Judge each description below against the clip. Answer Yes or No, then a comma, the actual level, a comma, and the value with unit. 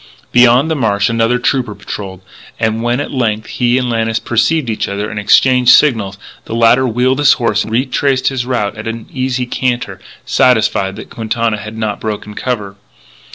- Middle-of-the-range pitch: No, low, 115 Hz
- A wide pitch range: No, average, 2.7 semitones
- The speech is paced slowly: No, average, 180 wpm